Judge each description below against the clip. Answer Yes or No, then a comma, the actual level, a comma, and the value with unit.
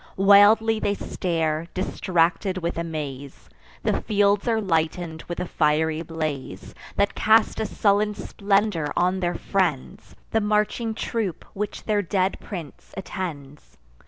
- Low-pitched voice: No, medium, 185 Hz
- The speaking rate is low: Yes, slow, 130 wpm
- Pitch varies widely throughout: No, average, 4.3 semitones